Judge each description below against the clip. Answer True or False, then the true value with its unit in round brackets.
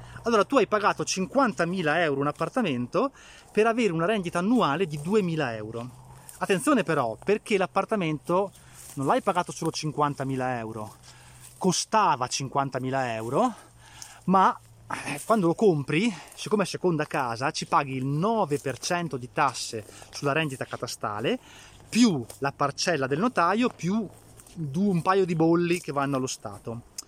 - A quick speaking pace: False (135 wpm)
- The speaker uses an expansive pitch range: True (6.5 semitones)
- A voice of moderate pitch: True (155 Hz)